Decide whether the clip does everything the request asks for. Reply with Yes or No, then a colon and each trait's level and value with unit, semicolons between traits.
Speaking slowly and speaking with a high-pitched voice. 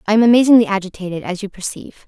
No: average, 200 wpm; high, 205 Hz